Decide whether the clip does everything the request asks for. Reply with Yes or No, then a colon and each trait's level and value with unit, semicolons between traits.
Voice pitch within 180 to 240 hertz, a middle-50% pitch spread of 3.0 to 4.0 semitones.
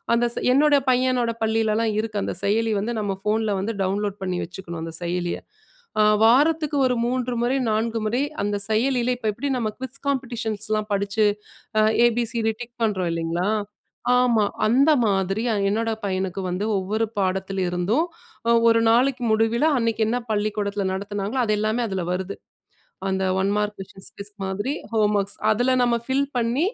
Yes: high, 215 Hz; average, 3.4 semitones